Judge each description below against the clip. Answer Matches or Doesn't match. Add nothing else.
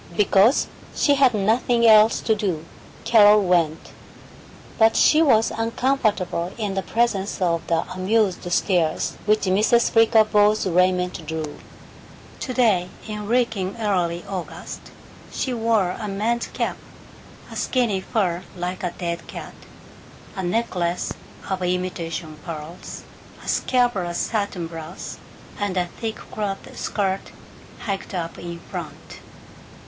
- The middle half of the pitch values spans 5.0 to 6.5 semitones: Doesn't match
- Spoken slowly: Matches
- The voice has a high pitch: Matches